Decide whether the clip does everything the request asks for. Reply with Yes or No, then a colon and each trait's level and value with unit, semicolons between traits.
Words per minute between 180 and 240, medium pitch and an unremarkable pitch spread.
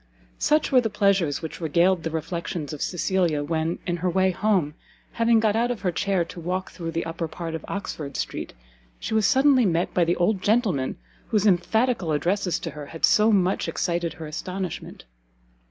Yes: average, 185 wpm; medium, 180 Hz; average, 3.8 semitones